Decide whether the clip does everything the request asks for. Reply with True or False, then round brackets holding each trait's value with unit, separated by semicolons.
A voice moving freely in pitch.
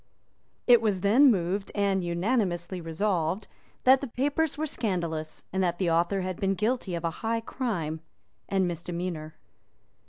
False (4.7 semitones)